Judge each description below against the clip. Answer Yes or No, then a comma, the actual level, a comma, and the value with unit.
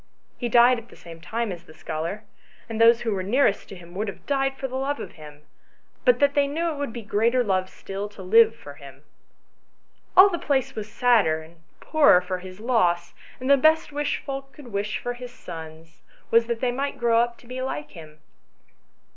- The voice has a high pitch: Yes, high, 230 Hz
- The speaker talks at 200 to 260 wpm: Yes, fast, 205 wpm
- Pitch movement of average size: No, wide, 6.4 semitones